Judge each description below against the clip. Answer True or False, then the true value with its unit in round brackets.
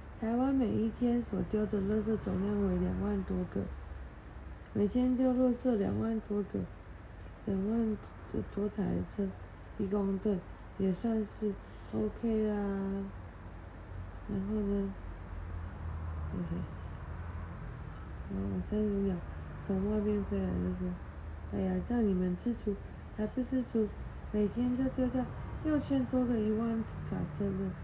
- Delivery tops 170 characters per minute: False (165 characters per minute)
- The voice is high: True (195 Hz)